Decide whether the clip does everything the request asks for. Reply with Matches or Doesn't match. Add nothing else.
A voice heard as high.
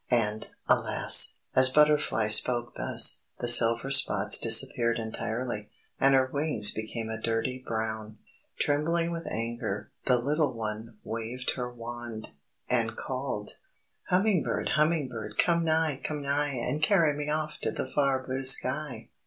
Doesn't match